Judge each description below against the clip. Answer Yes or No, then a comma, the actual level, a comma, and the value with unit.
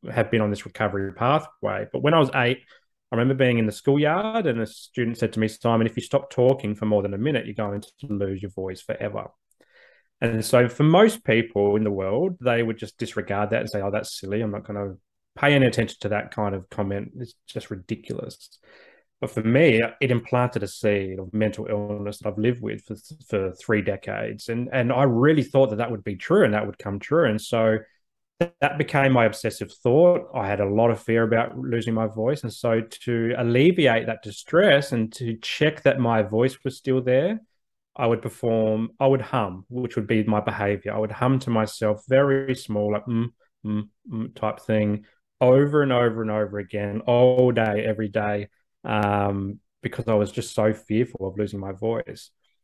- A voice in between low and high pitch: No, low, 115 Hz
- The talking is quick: Yes, fast, 210 wpm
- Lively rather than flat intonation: No, average, 3.3 semitones